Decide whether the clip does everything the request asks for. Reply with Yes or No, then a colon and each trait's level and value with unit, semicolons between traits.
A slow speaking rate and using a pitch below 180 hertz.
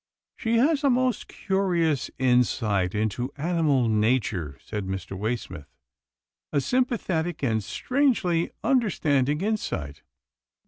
Yes: slow, 110 wpm; medium, 140 Hz